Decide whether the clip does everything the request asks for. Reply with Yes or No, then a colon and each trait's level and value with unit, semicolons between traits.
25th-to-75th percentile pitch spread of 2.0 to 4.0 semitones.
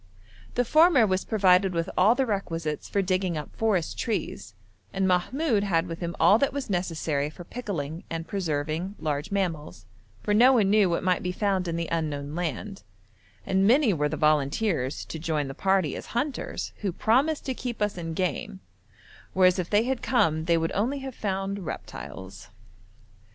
No: average, 4.6 semitones